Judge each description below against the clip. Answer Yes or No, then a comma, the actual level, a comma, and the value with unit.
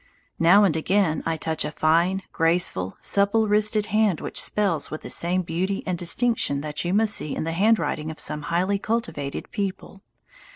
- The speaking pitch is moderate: Yes, medium, 180 Hz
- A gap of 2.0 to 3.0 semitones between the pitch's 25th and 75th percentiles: No, average, 4.3 semitones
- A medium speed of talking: Yes, average, 175 wpm